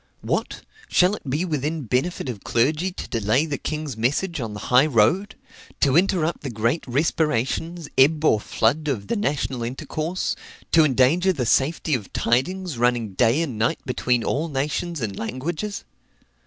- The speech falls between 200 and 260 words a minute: No, average, 160 wpm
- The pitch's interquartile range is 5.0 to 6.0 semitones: Yes, average, 5.3 semitones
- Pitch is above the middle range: No, medium, 140 Hz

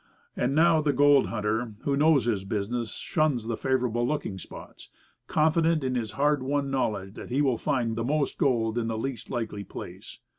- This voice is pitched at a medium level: No, low, 125 Hz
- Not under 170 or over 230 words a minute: Yes, average, 185 wpm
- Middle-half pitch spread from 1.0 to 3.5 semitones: No, average, 4.3 semitones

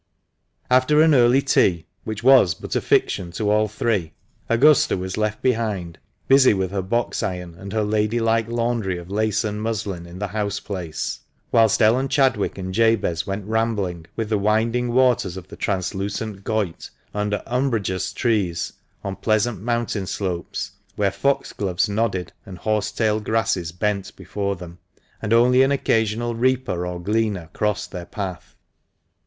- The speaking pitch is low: Yes, low, 105 Hz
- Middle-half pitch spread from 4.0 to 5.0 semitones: No, average, 3.4 semitones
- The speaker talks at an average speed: Yes, average, 155 wpm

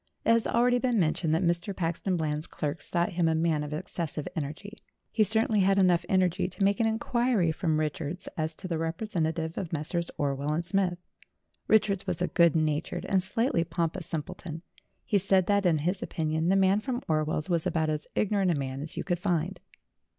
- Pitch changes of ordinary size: Yes, average, 3.6 semitones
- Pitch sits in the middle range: Yes, medium, 175 Hz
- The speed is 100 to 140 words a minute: No, average, 195 wpm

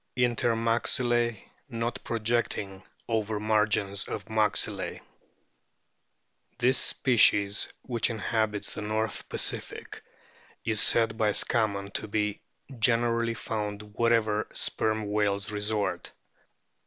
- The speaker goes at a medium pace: No, slow, 95 wpm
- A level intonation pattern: Yes, narrow, 1.9 semitones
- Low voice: Yes, low, 110 Hz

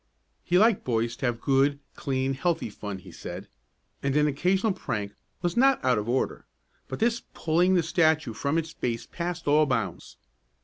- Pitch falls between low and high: Yes, medium, 145 Hz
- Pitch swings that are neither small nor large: No, wide, 6.2 semitones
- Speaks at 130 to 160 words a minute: No, average, 175 wpm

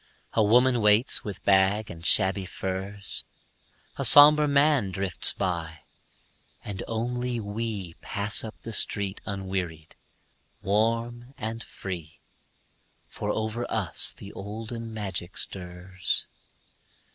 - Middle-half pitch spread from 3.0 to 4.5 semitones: Yes, average, 3.3 semitones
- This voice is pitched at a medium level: No, low, 105 Hz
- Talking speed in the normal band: No, slow, 110 wpm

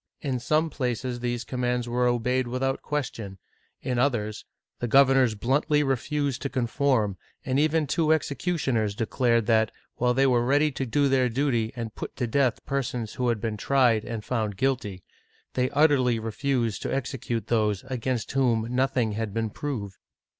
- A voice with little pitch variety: No, average, 3.1 semitones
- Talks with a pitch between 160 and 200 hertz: No, low, 125 Hz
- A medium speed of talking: Yes, average, 160 wpm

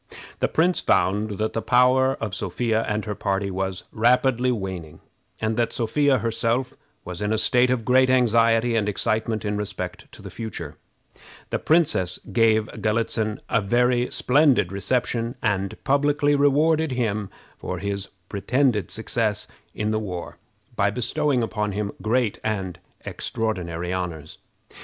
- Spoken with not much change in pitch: No, average, 3.8 semitones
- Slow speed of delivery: No, average, 145 wpm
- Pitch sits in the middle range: No, low, 110 Hz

